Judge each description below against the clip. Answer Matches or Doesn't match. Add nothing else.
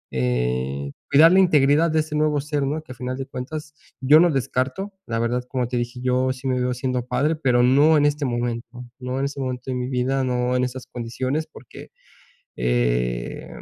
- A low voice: Matches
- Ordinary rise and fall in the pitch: Matches